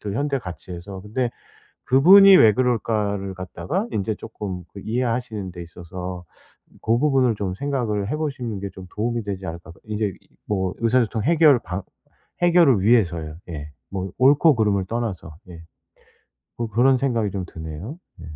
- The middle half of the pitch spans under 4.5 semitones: No, average, 5.3 semitones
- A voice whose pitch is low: Yes, low, 105 Hz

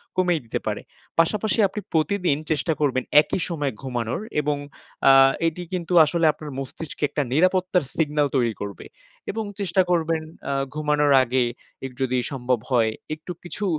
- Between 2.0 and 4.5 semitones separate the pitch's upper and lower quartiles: No, average, 4.9 semitones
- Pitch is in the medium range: Yes, medium, 155 Hz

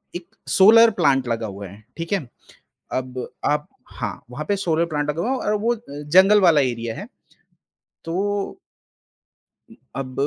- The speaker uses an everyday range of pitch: No, wide, 7.3 semitones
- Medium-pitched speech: Yes, medium, 155 Hz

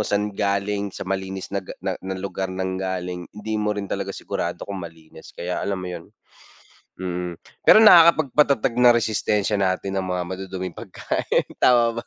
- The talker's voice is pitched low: Yes, very low, 95 Hz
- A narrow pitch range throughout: Yes, narrow, 2.2 semitones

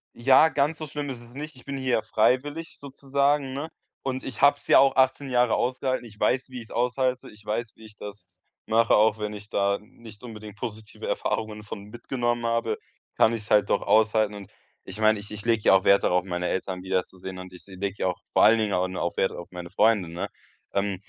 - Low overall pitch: Yes, low, 110 Hz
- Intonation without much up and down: No, average, 4.3 semitones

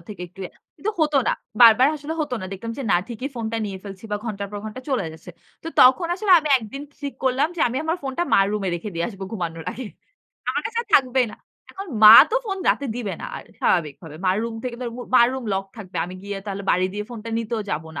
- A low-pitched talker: No, high, 230 Hz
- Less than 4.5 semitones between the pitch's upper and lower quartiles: No, average, 5.3 semitones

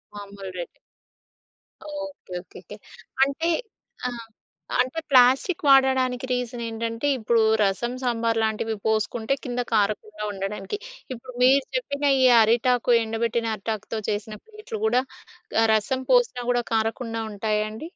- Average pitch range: Yes, average, 3.2 semitones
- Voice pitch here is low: No, high, 230 Hz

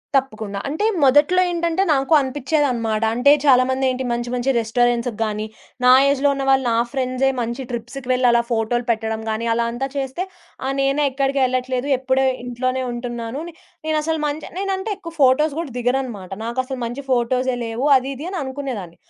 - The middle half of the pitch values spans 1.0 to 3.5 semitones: Yes, narrow, 2.6 semitones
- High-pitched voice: Yes, very high, 255 Hz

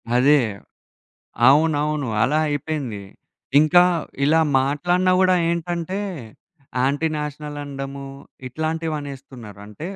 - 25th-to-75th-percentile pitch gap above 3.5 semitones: No, average, 2.8 semitones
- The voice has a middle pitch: Yes, medium, 150 Hz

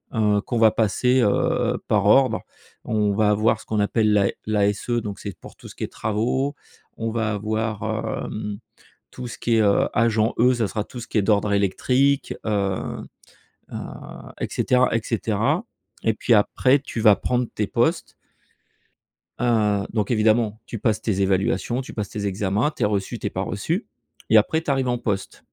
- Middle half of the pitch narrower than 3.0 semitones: Yes, narrow, 2.5 semitones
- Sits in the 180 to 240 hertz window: No, low, 110 Hz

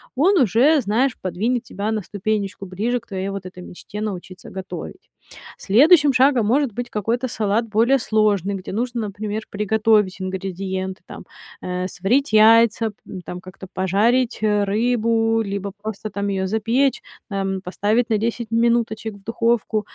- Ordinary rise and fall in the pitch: Yes, average, 3.0 semitones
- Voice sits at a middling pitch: No, high, 215 Hz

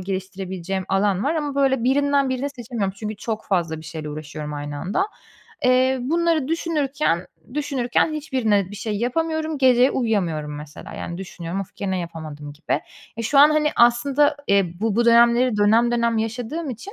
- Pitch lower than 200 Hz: No, high, 230 Hz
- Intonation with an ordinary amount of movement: No, wide, 6.5 semitones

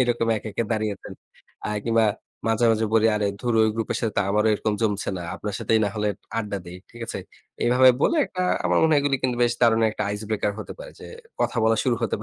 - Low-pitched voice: Yes, low, 115 Hz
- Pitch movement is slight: Yes, narrow, 2.1 semitones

